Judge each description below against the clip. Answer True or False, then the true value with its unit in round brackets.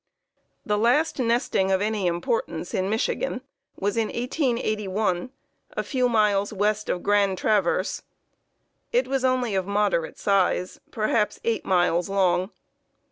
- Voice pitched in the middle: False (210 Hz)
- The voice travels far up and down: False (3.5 semitones)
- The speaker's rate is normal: False (130 wpm)